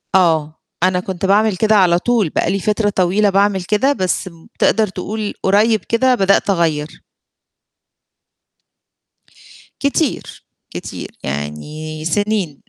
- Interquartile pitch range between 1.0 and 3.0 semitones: No, average, 3.8 semitones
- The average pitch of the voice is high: Yes, high, 195 Hz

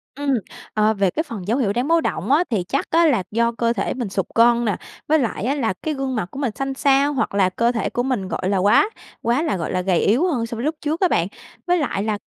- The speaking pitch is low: No, high, 235 Hz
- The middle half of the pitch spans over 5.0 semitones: Yes, wide, 5.6 semitones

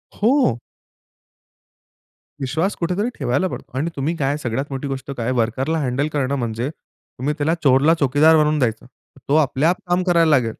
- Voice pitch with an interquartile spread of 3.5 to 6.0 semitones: Yes, average, 3.9 semitones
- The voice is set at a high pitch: No, medium, 145 Hz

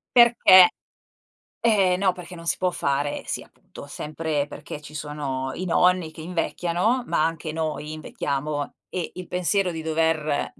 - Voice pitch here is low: No, medium, 165 Hz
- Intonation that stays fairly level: No, average, 3.3 semitones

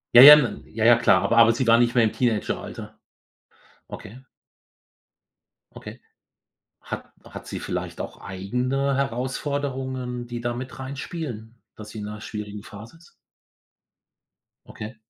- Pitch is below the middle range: Yes, low, 120 Hz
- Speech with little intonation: No, average, 3.1 semitones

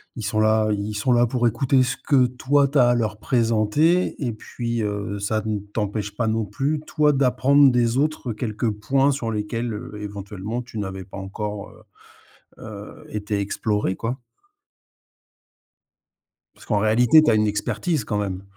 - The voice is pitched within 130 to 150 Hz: No, low, 110 Hz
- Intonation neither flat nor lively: Yes, average, 3.3 semitones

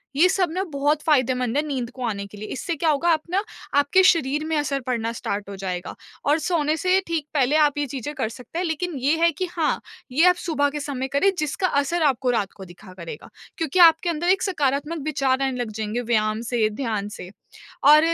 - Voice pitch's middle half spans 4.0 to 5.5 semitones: Yes, average, 5.1 semitones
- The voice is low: No, very high, 285 Hz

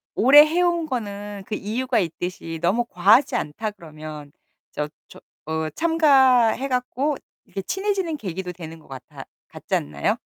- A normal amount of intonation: No, wide, 8.7 semitones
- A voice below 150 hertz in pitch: No, high, 210 Hz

